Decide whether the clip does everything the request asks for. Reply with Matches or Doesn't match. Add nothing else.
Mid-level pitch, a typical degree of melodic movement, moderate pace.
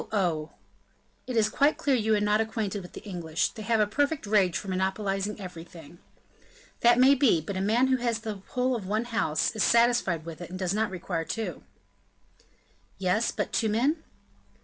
Doesn't match